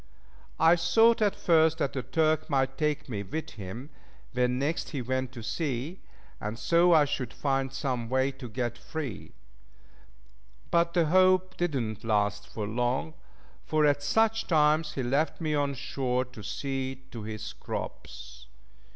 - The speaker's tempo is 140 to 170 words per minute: Yes, average, 155 wpm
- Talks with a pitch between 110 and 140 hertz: Yes, low, 135 Hz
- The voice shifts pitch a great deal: No, average, 4.6 semitones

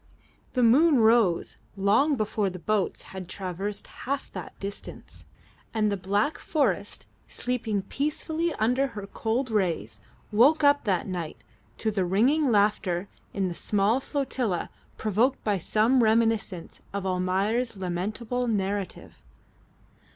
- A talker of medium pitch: No, high, 210 Hz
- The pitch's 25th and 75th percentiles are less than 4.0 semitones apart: No, average, 4.4 semitones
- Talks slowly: Yes, slow, 125 wpm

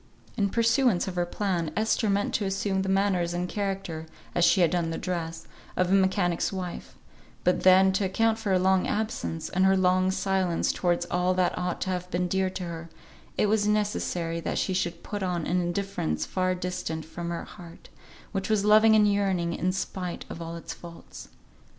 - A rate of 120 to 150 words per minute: No, average, 195 wpm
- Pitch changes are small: Yes, narrow, 2.2 semitones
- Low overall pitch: No, medium, 185 Hz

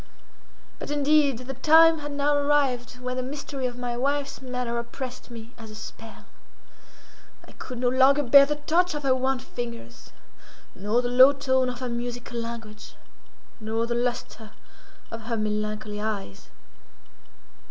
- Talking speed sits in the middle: Yes, average, 150 wpm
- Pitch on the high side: Yes, very high, 250 Hz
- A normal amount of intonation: Yes, average, 3.2 semitones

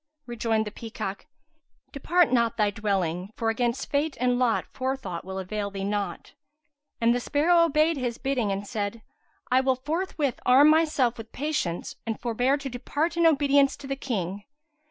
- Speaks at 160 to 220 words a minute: Yes, average, 165 wpm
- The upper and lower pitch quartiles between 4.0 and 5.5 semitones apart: Yes, average, 4.9 semitones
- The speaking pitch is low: No, high, 245 Hz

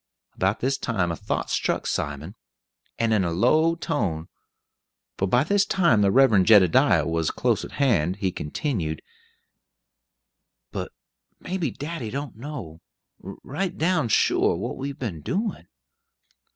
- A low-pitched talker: Yes, low, 115 Hz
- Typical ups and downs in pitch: No, wide, 8.4 semitones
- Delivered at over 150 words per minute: No, average, 140 wpm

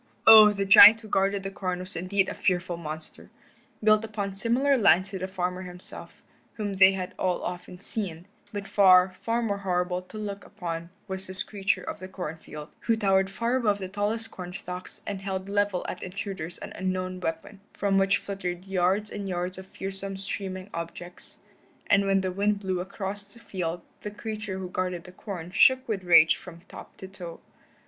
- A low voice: No, high, 190 Hz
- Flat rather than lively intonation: Yes, narrow, 2.0 semitones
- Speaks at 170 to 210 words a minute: Yes, average, 190 wpm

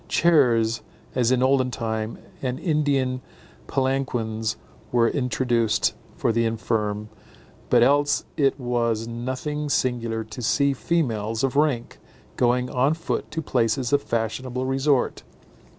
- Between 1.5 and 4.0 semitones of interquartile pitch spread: Yes, average, 3.0 semitones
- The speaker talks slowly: Yes, slow, 120 wpm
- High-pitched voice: No, low, 125 Hz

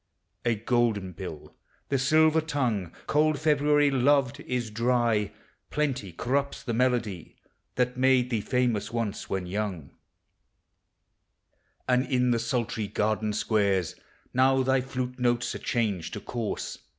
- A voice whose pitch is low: Yes, low, 120 Hz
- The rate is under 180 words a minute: Yes, slow, 135 wpm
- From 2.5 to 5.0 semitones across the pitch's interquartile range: Yes, average, 3.8 semitones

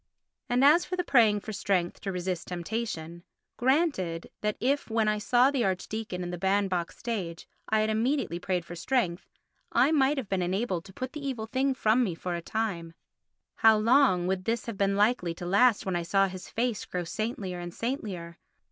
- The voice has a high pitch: Yes, high, 205 Hz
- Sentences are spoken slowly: No, average, 190 wpm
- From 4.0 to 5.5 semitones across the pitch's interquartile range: Yes, average, 5.2 semitones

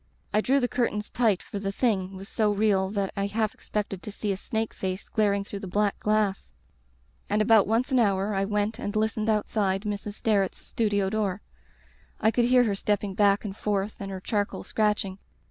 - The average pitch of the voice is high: Yes, high, 205 Hz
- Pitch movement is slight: Yes, narrow, 1.6 semitones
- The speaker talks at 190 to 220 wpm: Yes, average, 195 wpm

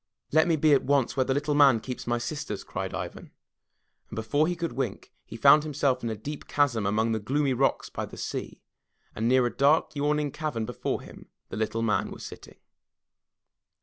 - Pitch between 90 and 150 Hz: Yes, low, 135 Hz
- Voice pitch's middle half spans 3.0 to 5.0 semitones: Yes, average, 4.5 semitones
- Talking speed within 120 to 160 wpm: No, average, 200 wpm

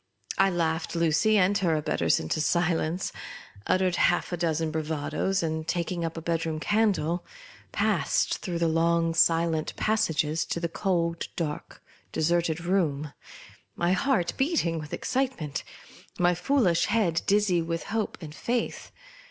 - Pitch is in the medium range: Yes, medium, 170 Hz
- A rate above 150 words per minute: No, average, 145 wpm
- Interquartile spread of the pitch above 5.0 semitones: No, narrow, 2.6 semitones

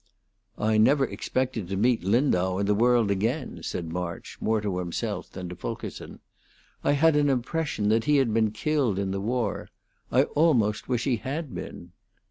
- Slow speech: No, average, 175 wpm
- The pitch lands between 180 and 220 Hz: No, low, 110 Hz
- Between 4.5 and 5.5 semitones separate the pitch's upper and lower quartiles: Yes, average, 5.1 semitones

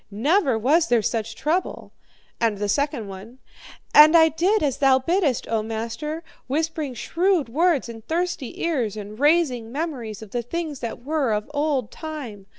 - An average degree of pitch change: No, wide, 6.0 semitones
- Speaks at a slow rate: No, average, 165 wpm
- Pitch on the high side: Yes, very high, 275 Hz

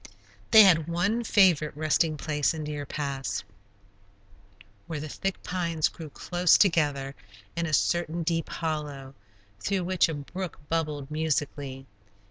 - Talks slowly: Yes, slow, 130 wpm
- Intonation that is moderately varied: Yes, average, 3.0 semitones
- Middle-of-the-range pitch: Yes, medium, 155 Hz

